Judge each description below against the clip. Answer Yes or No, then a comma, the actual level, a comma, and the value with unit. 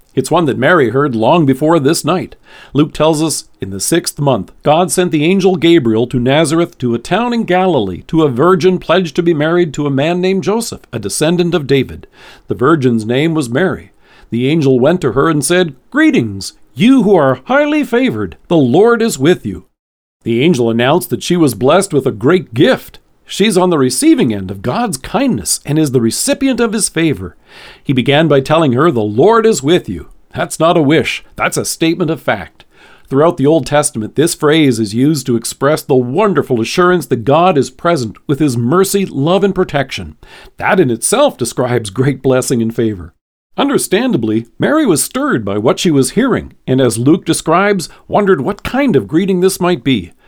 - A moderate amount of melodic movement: No, wide, 6.2 semitones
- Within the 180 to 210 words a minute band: Yes, average, 195 wpm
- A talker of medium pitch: Yes, medium, 155 Hz